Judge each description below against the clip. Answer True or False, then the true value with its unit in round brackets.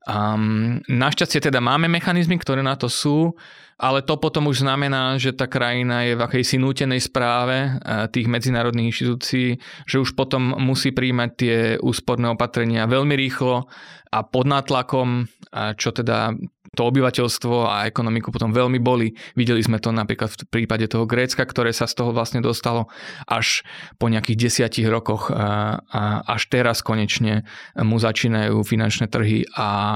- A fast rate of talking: False (150 wpm)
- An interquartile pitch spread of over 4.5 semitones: False (2.6 semitones)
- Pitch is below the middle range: True (120 Hz)